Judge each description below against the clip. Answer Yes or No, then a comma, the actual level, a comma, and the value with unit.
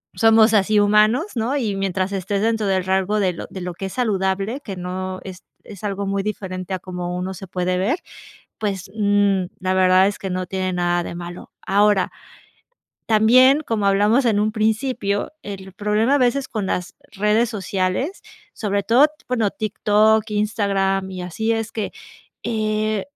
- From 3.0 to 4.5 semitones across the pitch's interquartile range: No, narrow, 2.5 semitones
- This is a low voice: No, high, 200 Hz